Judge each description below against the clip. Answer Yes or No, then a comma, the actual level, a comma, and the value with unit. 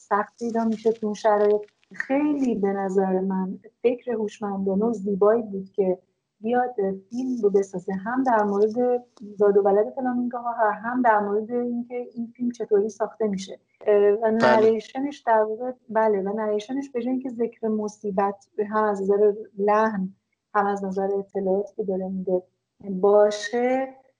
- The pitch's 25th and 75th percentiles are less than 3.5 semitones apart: Yes, average, 2.8 semitones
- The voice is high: Yes, high, 215 Hz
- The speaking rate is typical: Yes, average, 145 wpm